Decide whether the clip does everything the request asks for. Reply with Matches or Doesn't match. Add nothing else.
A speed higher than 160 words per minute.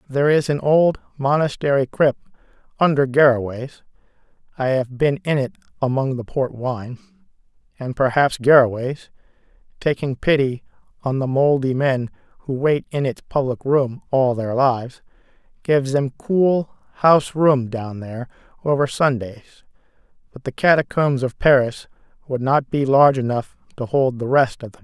Doesn't match